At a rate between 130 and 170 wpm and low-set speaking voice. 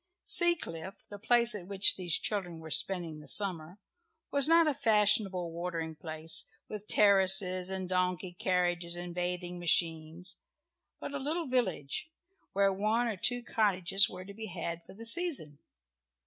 No: average, 150 wpm; medium, 185 Hz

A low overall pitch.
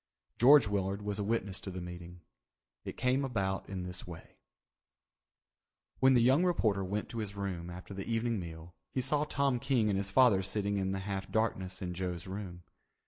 Yes: low, 100 Hz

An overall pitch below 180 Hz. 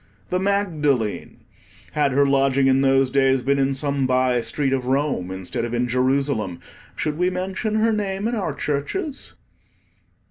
Yes: medium, 140 Hz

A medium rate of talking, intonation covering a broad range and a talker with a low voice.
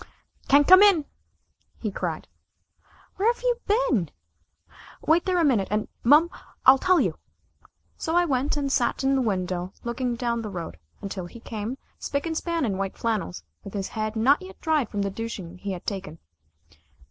No: average, 175 wpm; wide, 8.2 semitones; high, 240 Hz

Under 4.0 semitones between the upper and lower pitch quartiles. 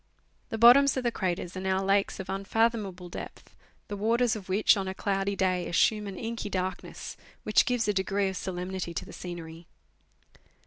Yes: average, 2.8 semitones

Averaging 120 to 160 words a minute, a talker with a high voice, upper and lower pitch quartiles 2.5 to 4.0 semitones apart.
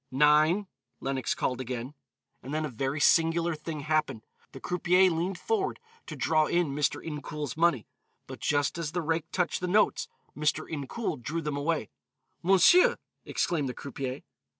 No: average, 155 wpm; medium, 155 Hz; average, 3.4 semitones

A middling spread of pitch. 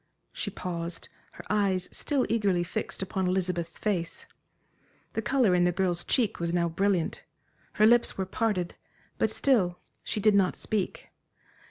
Yes: average, 3.3 semitones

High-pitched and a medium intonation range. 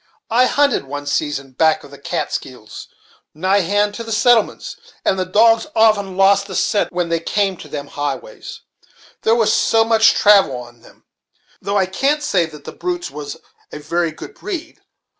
No: high, 200 Hz; wide, 6.0 semitones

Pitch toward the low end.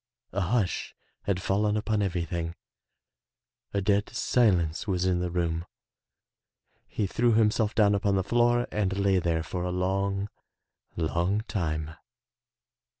Yes: very low, 95 Hz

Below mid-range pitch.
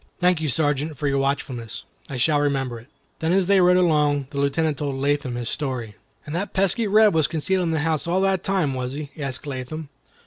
No: medium, 150 Hz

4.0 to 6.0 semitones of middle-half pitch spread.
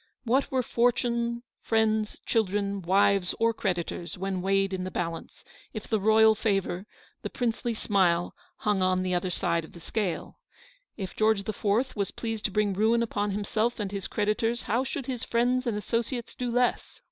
No: average, 3.3 semitones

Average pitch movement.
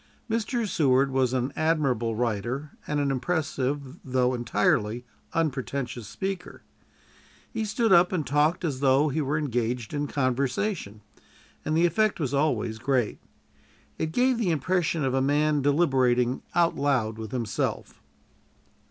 Yes: average, 4.4 semitones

